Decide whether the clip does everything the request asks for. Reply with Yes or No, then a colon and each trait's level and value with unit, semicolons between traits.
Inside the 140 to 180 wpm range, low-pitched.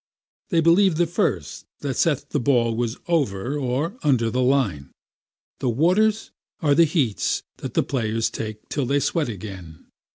Yes: average, 160 wpm; low, 130 Hz